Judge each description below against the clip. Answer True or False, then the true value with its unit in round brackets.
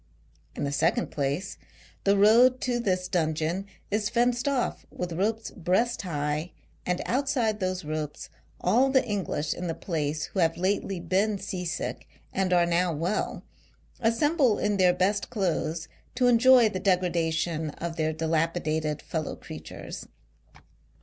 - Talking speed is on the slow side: False (145 wpm)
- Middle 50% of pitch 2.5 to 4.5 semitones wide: False (5.0 semitones)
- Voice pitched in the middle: True (180 Hz)